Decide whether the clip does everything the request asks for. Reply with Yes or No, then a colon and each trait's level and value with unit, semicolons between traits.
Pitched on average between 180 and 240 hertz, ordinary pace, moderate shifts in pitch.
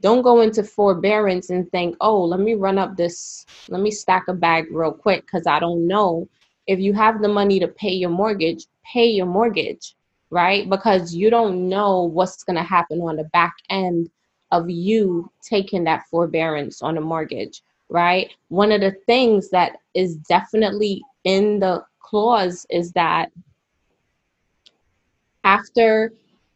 Yes: medium, 185 Hz; average, 160 wpm; average, 3.4 semitones